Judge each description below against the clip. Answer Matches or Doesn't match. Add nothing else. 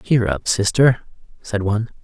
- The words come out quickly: Doesn't match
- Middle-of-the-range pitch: Doesn't match